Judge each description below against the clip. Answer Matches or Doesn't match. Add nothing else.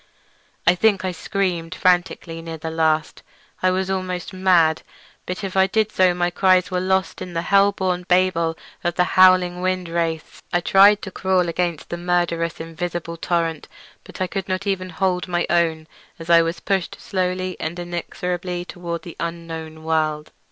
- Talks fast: Doesn't match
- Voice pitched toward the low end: Doesn't match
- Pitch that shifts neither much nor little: Doesn't match